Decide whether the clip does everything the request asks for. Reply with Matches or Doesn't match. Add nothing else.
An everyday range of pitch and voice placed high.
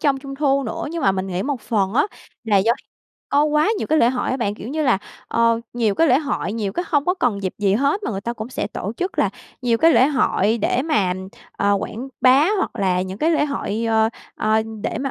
Doesn't match